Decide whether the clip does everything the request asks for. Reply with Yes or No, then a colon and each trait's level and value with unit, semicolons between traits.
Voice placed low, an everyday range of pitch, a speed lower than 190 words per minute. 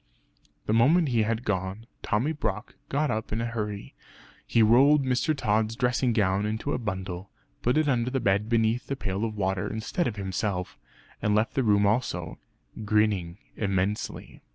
Yes: low, 110 Hz; average, 3.4 semitones; average, 170 wpm